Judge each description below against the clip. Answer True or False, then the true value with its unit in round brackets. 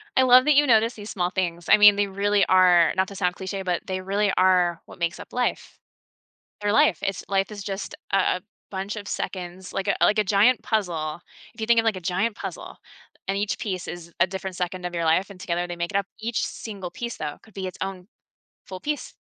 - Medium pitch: False (195 Hz)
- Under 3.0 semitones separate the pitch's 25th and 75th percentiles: True (2.5 semitones)